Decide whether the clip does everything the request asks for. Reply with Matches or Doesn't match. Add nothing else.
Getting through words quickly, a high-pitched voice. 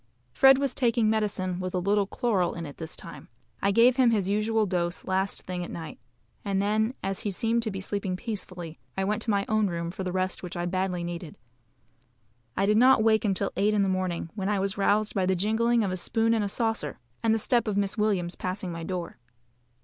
Matches